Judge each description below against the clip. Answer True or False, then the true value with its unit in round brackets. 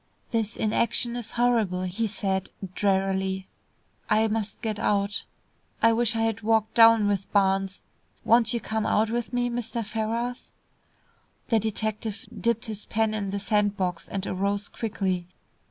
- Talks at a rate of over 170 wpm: False (150 wpm)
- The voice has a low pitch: False (215 Hz)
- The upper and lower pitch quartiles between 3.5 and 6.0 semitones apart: False (2.4 semitones)